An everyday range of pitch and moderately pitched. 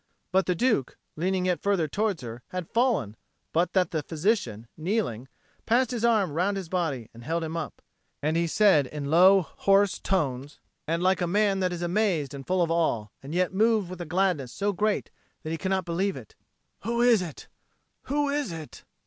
Yes: average, 4.3 semitones; medium, 180 Hz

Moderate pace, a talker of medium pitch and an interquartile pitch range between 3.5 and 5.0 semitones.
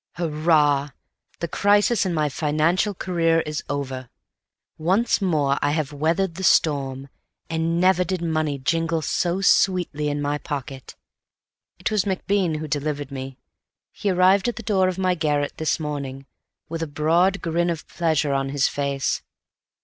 Yes: average, 155 wpm; medium, 160 Hz; average, 3.9 semitones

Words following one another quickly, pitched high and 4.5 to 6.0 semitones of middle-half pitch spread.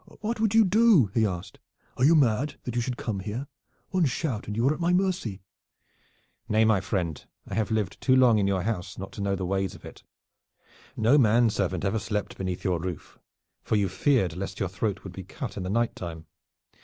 No: fast, 215 wpm; low, 105 Hz; average, 5.2 semitones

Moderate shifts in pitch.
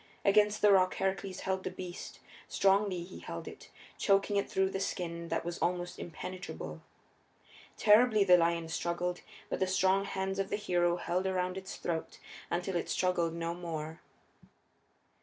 No: narrow, 2.0 semitones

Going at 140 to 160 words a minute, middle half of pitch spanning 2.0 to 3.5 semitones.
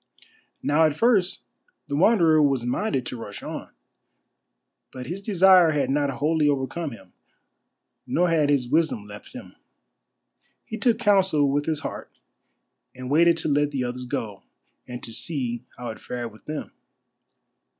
No: average, 150 wpm; average, 5.1 semitones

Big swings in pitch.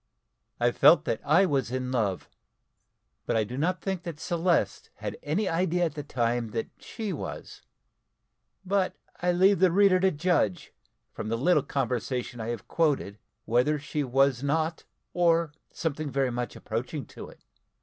Yes: wide, 6.0 semitones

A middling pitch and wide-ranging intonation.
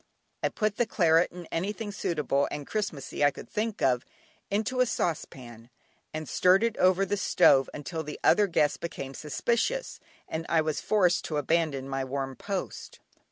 Yes: medium, 165 Hz; wide, 6.3 semitones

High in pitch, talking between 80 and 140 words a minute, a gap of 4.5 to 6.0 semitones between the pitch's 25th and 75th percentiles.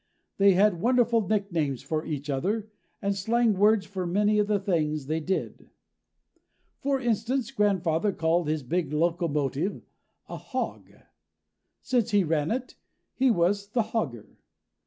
Yes: high, 195 Hz; slow, 135 wpm; average, 5.0 semitones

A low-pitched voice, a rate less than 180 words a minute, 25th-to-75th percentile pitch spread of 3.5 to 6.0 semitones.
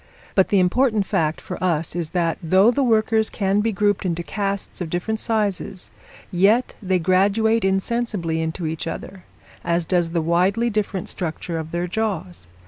No: high, 190 Hz; average, 165 wpm; average, 3.8 semitones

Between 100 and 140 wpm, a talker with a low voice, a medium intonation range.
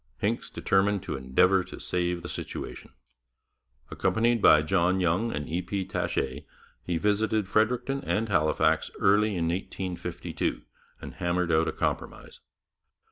Yes: slow, 135 wpm; very low, 90 Hz; average, 3.4 semitones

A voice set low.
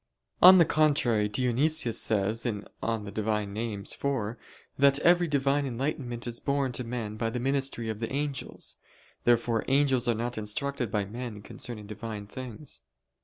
Yes: low, 120 Hz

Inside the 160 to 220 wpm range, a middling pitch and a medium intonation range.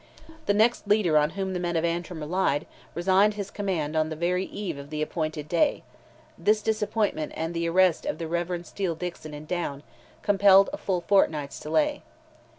Yes: average, 180 wpm; medium, 175 Hz; average, 4.0 semitones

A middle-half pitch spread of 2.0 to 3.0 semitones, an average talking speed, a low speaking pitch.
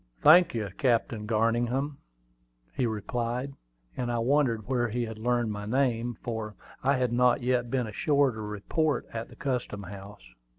Yes: average, 2.7 semitones; average, 160 wpm; low, 120 Hz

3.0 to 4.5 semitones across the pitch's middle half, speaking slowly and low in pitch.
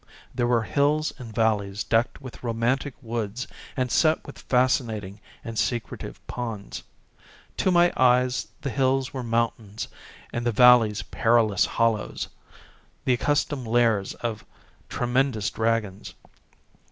No: narrow, 2.4 semitones; slow, 120 wpm; low, 120 Hz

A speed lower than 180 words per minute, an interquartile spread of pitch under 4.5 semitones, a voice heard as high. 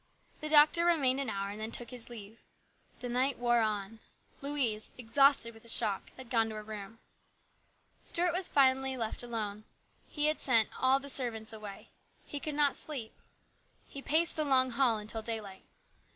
Yes: average, 170 wpm; average, 4.1 semitones; high, 240 Hz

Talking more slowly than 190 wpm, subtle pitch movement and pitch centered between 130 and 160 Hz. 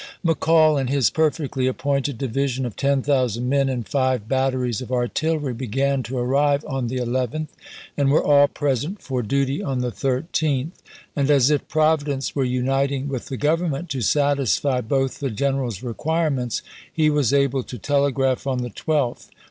Yes: average, 165 wpm; narrow, 2.2 semitones; low, 135 Hz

